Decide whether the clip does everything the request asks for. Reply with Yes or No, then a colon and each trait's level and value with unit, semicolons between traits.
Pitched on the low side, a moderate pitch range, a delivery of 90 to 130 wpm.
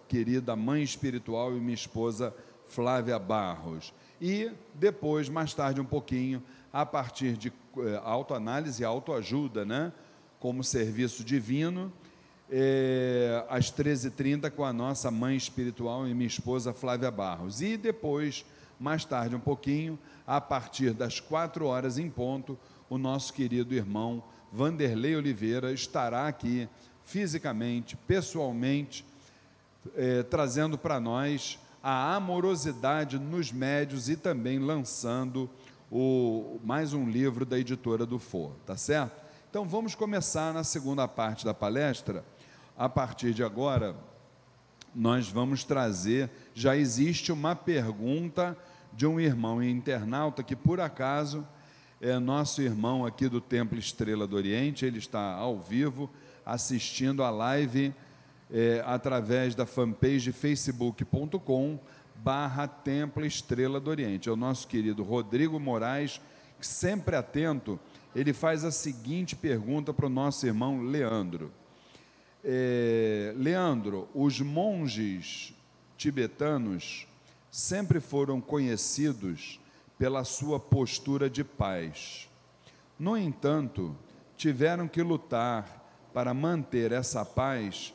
Yes: low, 130 Hz; average, 3.3 semitones; slow, 120 wpm